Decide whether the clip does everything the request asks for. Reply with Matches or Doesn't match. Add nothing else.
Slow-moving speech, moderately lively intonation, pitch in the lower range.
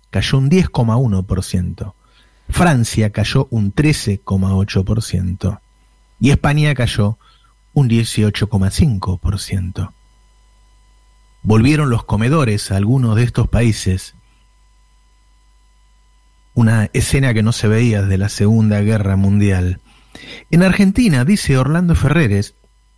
Matches